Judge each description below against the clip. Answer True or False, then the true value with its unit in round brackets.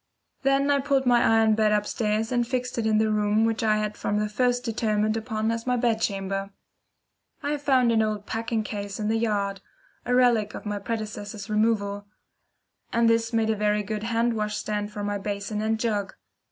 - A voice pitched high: True (220 Hz)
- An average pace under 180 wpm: False (195 wpm)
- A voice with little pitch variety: True (1.7 semitones)